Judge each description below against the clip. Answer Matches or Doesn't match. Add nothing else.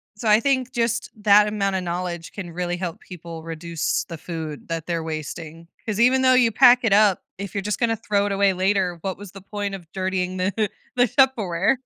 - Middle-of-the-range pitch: Doesn't match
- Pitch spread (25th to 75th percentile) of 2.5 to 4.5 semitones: Matches